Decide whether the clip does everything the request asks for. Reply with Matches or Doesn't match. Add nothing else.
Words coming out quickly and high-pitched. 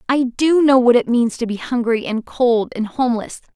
Matches